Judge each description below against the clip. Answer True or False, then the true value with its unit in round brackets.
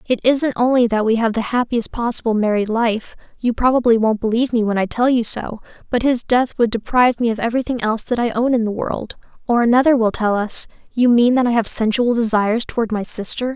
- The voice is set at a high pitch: True (230 Hz)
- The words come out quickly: True (225 wpm)